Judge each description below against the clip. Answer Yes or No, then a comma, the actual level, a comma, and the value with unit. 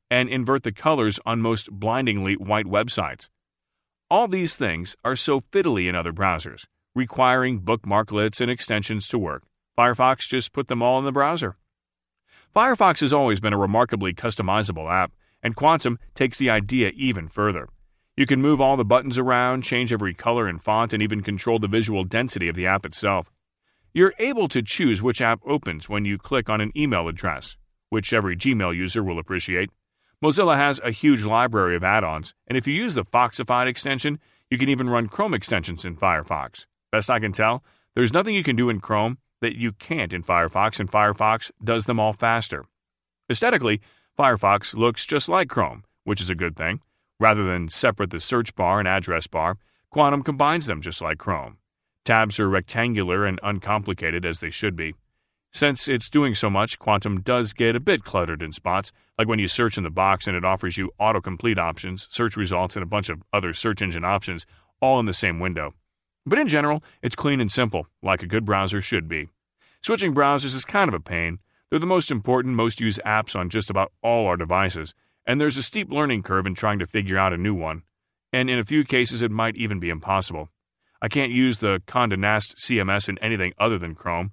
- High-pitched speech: No, low, 110 Hz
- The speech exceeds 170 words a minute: Yes, average, 200 wpm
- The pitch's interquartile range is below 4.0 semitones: No, average, 4.8 semitones